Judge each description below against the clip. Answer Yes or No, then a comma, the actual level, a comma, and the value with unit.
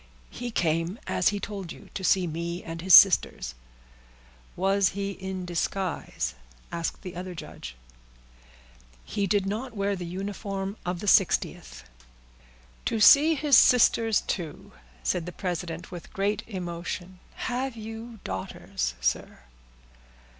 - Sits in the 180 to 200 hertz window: Yes, high, 190 Hz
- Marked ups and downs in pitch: No, average, 3.2 semitones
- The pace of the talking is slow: Yes, slow, 130 wpm